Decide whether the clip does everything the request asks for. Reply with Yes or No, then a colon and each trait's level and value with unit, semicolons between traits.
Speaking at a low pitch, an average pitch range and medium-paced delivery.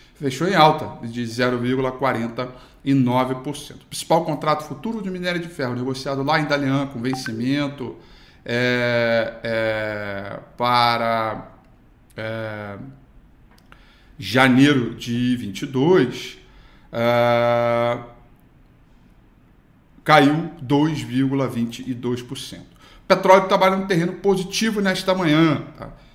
No: low, 130 Hz; average, 4.2 semitones; slow, 85 wpm